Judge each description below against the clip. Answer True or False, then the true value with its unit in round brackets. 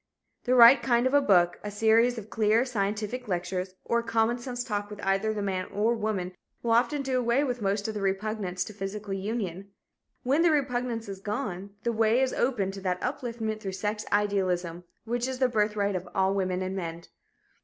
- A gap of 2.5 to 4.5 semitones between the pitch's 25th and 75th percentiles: True (3.5 semitones)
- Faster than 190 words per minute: True (200 wpm)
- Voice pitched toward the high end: True (210 Hz)